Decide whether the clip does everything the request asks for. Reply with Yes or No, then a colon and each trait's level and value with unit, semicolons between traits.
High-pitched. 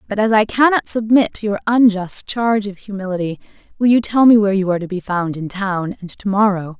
Yes: high, 205 Hz